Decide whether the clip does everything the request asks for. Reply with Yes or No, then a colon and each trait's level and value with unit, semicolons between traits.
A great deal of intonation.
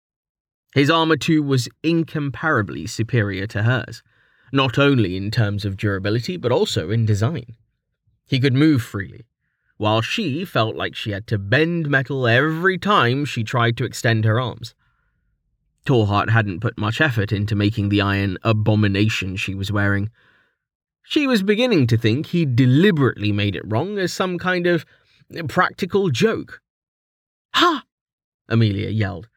Yes: wide, 6.1 semitones